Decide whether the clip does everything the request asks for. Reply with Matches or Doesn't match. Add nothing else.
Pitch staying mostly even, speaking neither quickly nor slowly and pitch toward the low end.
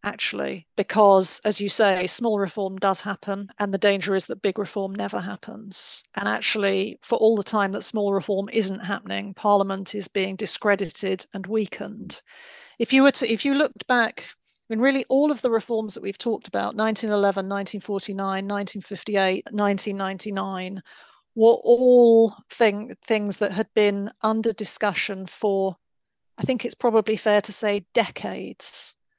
Doesn't match